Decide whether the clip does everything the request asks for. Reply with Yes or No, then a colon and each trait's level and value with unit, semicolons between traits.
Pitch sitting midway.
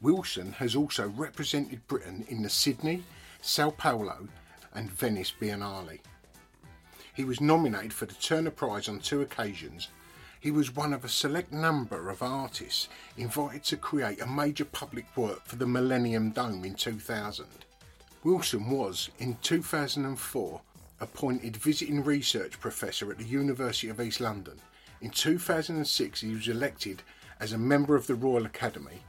No: low, 125 Hz